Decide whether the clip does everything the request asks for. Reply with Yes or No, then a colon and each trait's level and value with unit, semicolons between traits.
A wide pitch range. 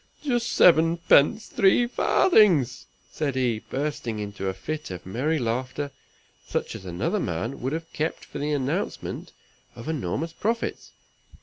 Yes: wide, 6.0 semitones